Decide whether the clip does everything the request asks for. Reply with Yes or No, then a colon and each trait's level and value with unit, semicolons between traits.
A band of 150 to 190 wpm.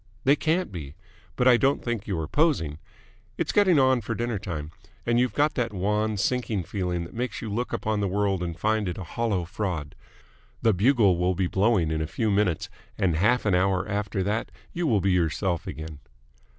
No: fast, 205 wpm